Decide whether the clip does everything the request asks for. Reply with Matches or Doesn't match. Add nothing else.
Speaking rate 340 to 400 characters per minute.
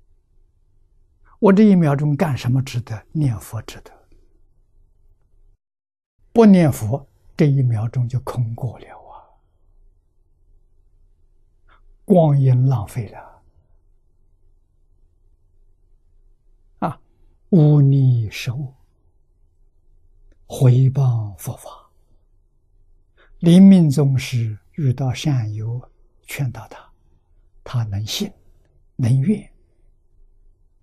Doesn't match